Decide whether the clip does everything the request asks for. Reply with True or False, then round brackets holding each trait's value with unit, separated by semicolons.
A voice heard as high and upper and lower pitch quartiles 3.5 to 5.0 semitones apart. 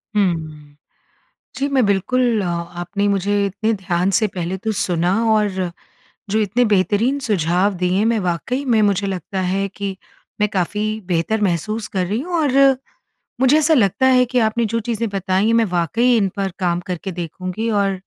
True (200 Hz; 3.8 semitones)